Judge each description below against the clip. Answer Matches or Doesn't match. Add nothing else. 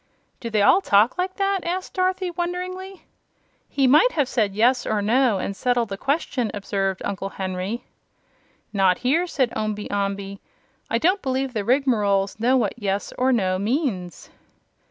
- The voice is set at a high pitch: Matches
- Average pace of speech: Matches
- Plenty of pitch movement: Matches